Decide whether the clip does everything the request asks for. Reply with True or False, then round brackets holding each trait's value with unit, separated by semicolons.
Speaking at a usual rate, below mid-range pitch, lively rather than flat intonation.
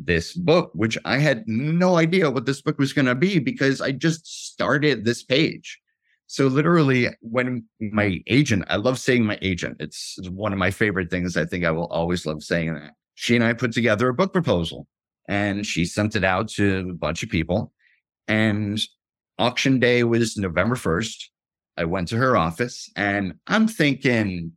True (190 wpm; 110 Hz; 6.6 semitones)